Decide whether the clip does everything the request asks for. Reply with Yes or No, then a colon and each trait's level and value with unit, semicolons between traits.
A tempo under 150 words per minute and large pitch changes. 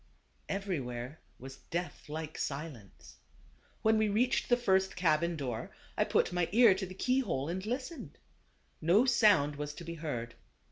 No: average, 155 wpm; wide, 5.9 semitones